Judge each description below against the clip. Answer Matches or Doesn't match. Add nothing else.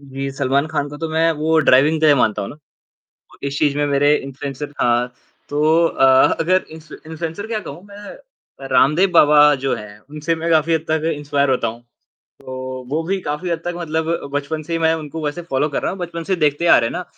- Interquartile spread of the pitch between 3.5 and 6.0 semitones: Doesn't match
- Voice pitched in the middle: Matches